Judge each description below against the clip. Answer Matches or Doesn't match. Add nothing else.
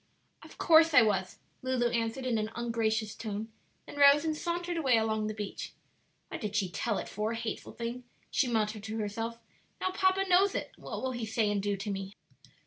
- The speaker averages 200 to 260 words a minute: Matches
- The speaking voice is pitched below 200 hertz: Doesn't match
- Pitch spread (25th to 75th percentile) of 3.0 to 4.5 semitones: Matches